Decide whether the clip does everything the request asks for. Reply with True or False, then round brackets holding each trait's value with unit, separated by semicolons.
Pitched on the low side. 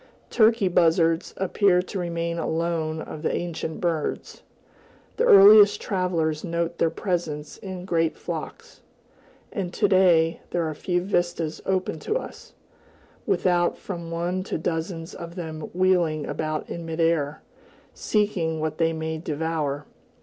False (170 Hz)